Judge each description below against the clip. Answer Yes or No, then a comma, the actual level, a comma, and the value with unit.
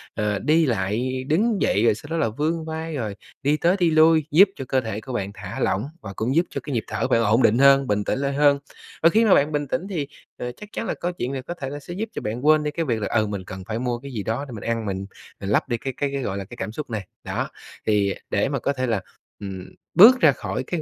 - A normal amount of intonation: No, wide, 6.2 semitones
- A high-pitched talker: No, low, 130 Hz